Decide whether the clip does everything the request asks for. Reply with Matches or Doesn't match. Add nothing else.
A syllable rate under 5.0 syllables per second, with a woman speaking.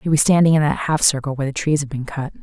Doesn't match